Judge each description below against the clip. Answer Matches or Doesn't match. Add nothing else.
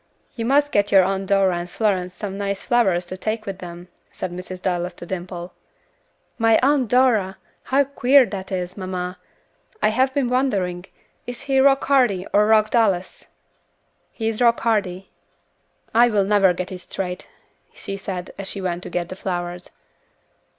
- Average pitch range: Matches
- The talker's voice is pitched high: Matches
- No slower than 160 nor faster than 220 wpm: Matches